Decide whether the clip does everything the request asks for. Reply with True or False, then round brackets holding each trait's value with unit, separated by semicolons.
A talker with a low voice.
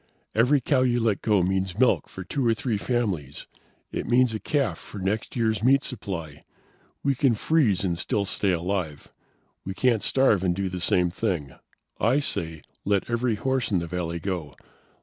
True (100 Hz)